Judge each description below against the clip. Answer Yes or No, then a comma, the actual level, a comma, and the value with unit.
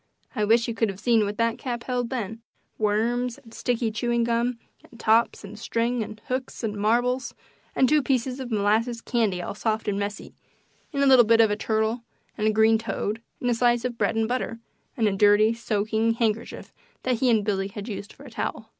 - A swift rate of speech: Yes, fast, 210 wpm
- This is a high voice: Yes, high, 230 Hz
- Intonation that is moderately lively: No, narrow, 2.1 semitones